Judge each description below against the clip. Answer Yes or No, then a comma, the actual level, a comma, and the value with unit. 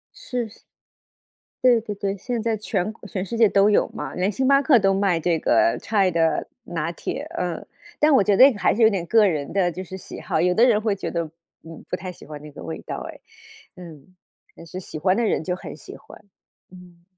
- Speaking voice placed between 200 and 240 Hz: No, high, 190 Hz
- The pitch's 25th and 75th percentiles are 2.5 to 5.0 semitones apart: Yes, average, 4.3 semitones